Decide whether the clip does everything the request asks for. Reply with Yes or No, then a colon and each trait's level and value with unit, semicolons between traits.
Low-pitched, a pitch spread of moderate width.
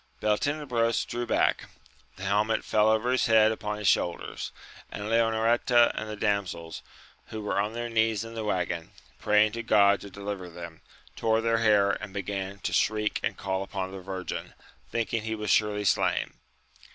No: low, 105 Hz; narrow, 2.2 semitones